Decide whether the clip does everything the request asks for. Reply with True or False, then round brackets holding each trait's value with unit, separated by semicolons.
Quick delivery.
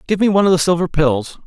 True (285 wpm)